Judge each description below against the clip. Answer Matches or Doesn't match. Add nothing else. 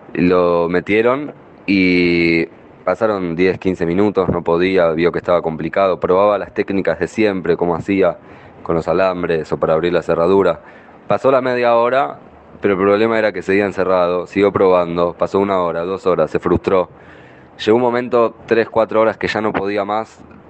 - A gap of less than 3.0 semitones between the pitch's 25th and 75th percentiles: Doesn't match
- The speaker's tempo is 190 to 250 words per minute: Doesn't match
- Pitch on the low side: Matches